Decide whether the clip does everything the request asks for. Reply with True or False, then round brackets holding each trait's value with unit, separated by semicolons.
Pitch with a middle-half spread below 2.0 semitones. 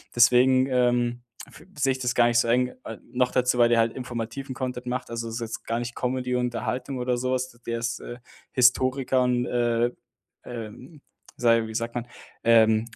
True (1.4 semitones)